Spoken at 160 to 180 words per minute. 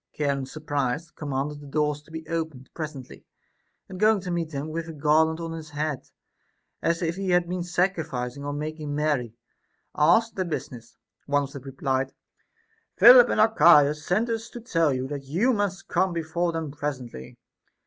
Yes: average, 175 wpm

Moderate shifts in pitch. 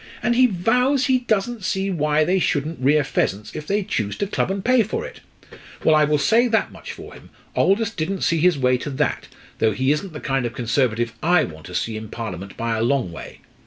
No: wide, 8.4 semitones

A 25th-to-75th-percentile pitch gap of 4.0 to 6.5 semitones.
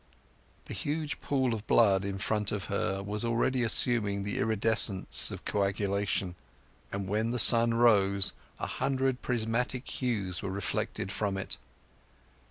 No: average, 3.3 semitones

